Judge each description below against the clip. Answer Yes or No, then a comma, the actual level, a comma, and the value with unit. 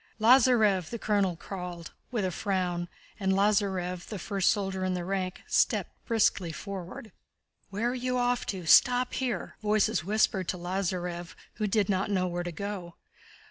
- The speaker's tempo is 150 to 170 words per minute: Yes, average, 160 wpm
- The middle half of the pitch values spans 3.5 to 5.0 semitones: No, average, 3.0 semitones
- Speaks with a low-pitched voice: No, high, 195 Hz